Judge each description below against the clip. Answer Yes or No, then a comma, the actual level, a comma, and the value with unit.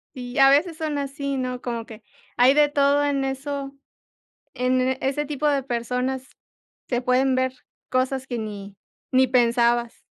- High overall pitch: Yes, very high, 260 Hz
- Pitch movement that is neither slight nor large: No, narrow, 2.1 semitones